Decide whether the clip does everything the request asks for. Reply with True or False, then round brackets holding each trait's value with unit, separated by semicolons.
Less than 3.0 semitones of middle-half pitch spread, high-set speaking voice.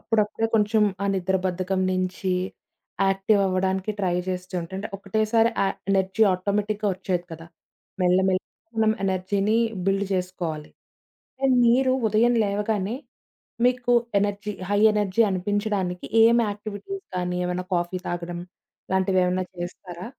True (2.4 semitones; 195 Hz)